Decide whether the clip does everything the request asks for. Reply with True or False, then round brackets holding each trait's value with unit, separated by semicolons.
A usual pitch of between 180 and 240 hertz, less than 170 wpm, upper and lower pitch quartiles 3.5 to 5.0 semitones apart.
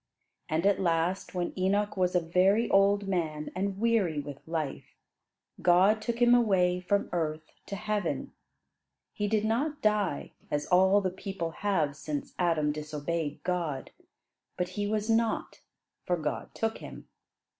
True (185 Hz; 145 wpm; 4.0 semitones)